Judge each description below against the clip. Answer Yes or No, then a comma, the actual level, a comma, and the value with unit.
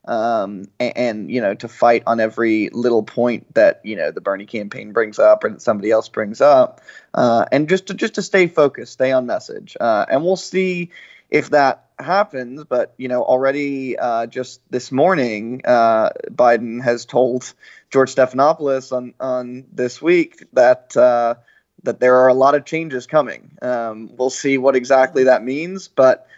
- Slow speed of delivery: No, average, 175 wpm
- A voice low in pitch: Yes, low, 130 Hz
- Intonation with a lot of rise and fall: No, average, 5.0 semitones